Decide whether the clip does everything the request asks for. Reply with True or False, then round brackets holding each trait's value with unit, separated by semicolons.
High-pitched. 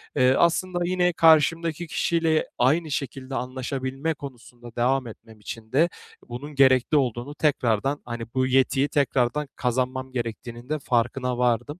False (130 Hz)